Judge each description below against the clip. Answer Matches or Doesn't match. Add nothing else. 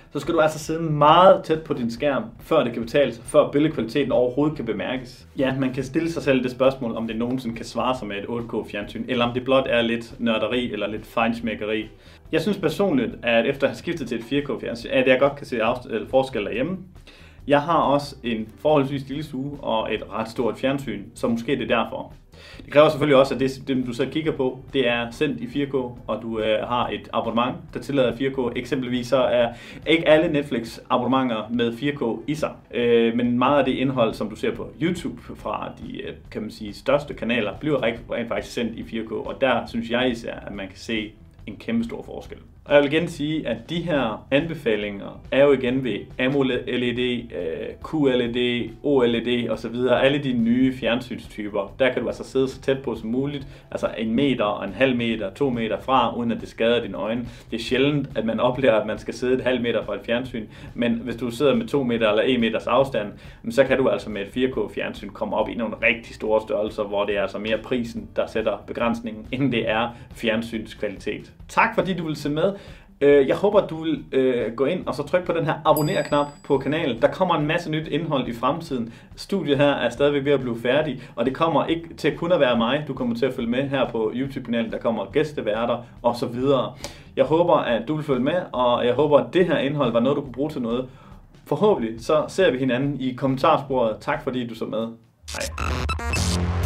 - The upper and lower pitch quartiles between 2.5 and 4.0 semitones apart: Matches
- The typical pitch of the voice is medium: Doesn't match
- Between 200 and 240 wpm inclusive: Matches